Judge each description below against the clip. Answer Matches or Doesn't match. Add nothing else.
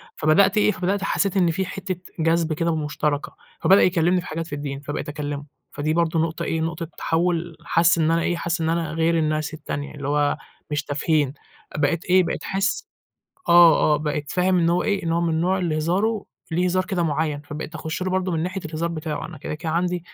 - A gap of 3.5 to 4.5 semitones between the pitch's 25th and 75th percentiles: Doesn't match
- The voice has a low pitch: Doesn't match